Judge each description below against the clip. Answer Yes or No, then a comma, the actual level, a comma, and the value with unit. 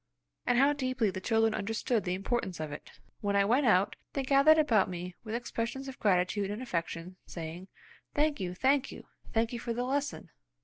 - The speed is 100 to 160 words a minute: No, average, 190 wpm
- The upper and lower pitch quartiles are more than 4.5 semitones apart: Yes, wide, 5.5 semitones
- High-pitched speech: Yes, high, 225 Hz